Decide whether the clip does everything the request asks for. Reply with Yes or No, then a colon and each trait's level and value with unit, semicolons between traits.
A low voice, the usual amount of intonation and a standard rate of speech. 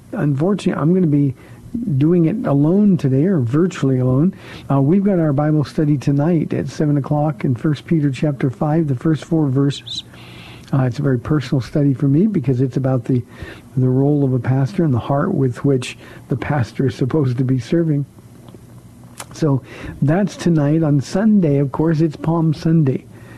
No: medium, 145 Hz; average, 3.3 semitones; average, 180 wpm